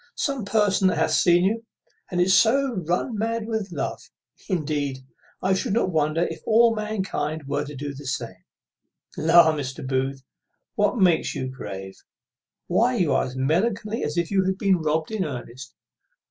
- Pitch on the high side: No, medium, 170 Hz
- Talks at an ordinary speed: Yes, average, 170 wpm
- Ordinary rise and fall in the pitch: No, wide, 6.6 semitones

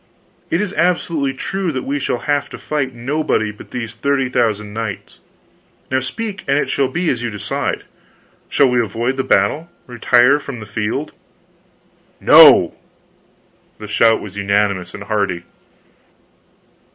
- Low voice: Yes, low, 125 Hz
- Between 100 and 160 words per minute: Yes, average, 145 wpm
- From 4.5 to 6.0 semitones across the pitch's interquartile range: Yes, average, 5.2 semitones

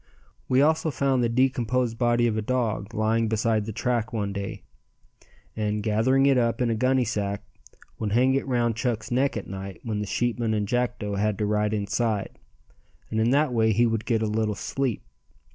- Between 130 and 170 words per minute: No, average, 190 wpm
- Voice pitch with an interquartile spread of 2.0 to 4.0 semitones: Yes, average, 2.7 semitones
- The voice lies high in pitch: No, low, 115 Hz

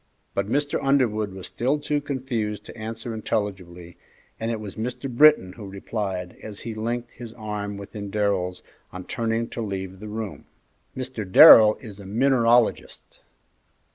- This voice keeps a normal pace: Yes, average, 150 wpm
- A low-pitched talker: Yes, low, 110 Hz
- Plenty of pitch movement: No, average, 3.1 semitones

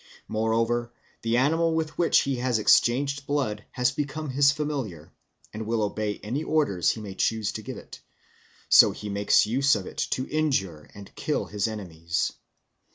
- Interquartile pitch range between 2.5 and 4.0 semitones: No, average, 5.1 semitones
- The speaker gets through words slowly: No, average, 165 wpm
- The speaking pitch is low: Yes, low, 120 Hz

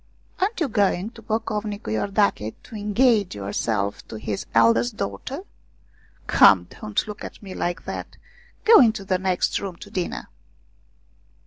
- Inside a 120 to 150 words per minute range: Yes, average, 140 wpm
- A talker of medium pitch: No, high, 195 Hz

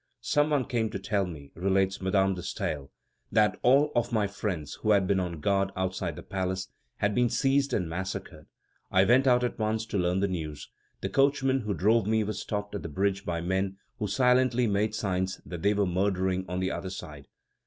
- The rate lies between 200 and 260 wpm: Yes, fast, 205 wpm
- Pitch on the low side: Yes, low, 100 Hz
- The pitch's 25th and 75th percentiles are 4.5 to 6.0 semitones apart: No, average, 3.0 semitones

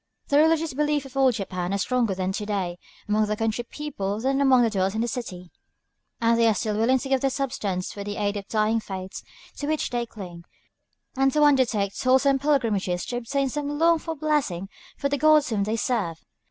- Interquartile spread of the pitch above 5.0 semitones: Yes, wide, 5.4 semitones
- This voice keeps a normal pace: No, fast, 210 wpm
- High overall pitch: Yes, high, 235 Hz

